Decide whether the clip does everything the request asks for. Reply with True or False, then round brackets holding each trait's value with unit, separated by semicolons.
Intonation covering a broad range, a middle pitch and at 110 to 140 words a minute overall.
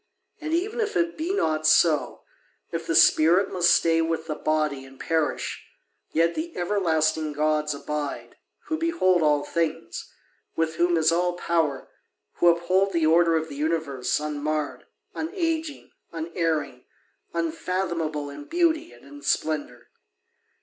False (3.3 semitones; 165 Hz; 135 wpm)